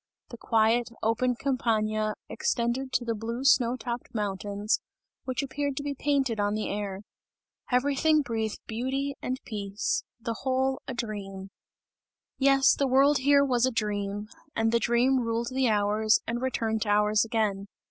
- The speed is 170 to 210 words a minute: No, average, 155 wpm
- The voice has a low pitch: No, high, 235 Hz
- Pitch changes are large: No, average, 3.5 semitones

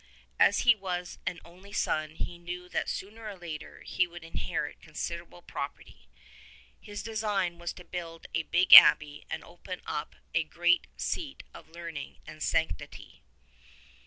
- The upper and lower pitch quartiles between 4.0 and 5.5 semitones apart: No, narrow, 2.6 semitones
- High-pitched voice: No, medium, 175 Hz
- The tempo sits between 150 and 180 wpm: Yes, average, 155 wpm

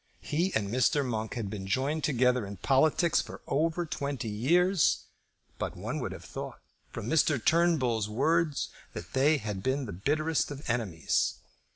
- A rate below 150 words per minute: No, average, 160 wpm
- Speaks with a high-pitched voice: No, low, 135 Hz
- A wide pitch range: Yes, wide, 5.9 semitones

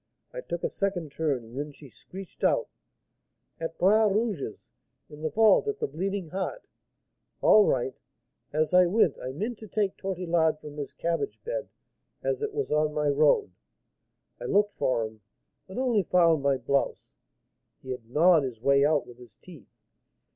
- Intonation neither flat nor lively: No, wide, 6.1 semitones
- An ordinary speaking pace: Yes, average, 170 wpm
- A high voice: No, medium, 165 Hz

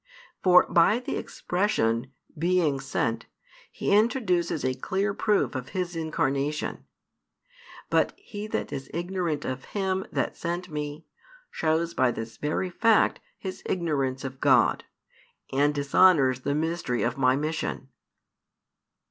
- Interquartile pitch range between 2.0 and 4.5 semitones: No, average, 5.3 semitones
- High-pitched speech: No, medium, 160 Hz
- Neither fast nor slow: No, slow, 125 wpm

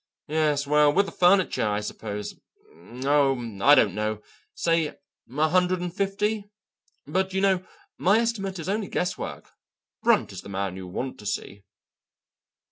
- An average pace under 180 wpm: Yes, average, 150 wpm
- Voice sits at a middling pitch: Yes, medium, 150 Hz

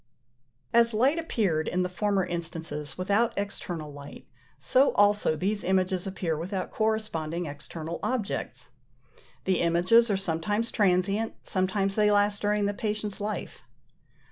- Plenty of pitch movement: No, average, 3.6 semitones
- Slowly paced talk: Yes, slow, 130 wpm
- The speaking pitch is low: No, high, 195 Hz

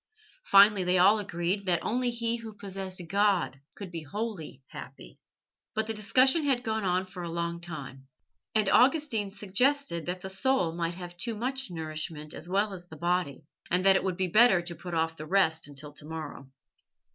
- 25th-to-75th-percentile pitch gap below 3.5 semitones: No, average, 4.2 semitones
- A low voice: No, medium, 185 Hz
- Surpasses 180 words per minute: Yes, average, 190 wpm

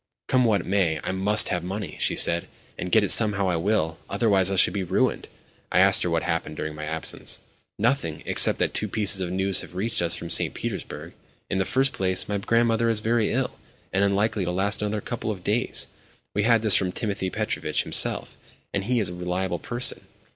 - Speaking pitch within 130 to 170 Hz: No, low, 100 Hz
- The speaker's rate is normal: No, fast, 210 wpm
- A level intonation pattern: No, average, 3.3 semitones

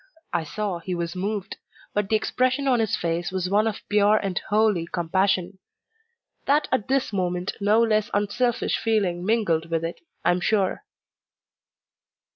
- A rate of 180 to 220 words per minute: No, average, 155 wpm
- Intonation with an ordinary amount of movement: Yes, average, 3.7 semitones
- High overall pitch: Yes, high, 200 Hz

